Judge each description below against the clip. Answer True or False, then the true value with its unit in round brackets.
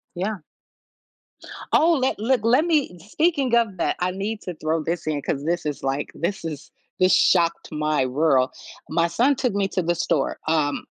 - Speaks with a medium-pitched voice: True (175 Hz)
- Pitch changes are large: True (6.3 semitones)